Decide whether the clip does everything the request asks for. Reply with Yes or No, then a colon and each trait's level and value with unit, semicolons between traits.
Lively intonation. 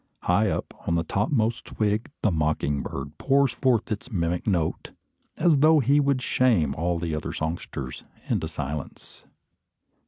Yes: wide, 8.0 semitones